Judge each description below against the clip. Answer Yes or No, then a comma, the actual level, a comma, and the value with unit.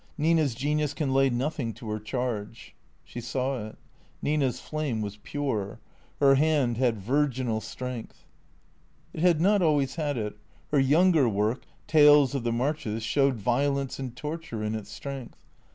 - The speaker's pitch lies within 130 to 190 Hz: Yes, low, 135 Hz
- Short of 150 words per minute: No, average, 160 wpm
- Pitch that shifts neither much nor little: Yes, average, 4.3 semitones